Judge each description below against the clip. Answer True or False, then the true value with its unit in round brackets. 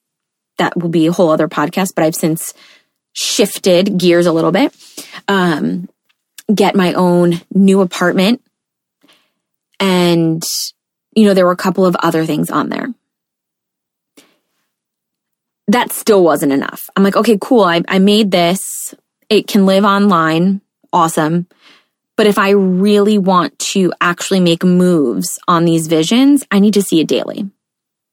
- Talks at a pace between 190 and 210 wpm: False (145 wpm)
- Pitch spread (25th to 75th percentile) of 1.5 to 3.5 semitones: True (3.2 semitones)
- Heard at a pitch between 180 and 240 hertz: True (185 Hz)